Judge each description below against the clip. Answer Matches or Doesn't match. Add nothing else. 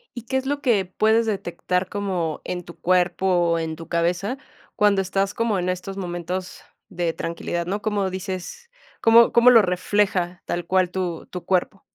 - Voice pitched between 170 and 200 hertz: Matches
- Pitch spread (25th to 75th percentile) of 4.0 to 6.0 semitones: Doesn't match